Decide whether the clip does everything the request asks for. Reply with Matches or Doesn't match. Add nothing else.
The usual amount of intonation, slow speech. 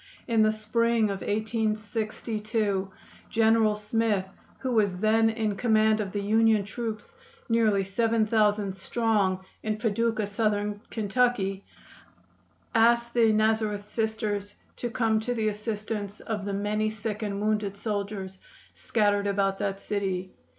Doesn't match